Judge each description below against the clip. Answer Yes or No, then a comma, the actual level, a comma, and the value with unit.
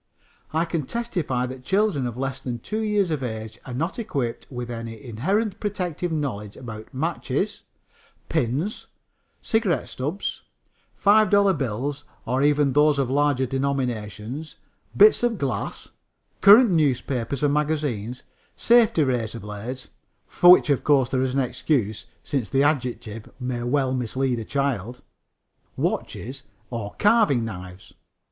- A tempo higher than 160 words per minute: No, slow, 135 wpm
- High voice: No, low, 135 Hz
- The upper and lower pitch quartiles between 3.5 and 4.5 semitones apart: No, average, 5.0 semitones